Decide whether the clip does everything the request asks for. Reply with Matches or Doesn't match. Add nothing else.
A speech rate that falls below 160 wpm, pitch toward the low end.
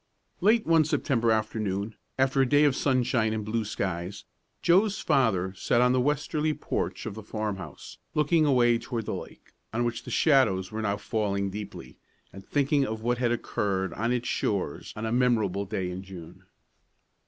Doesn't match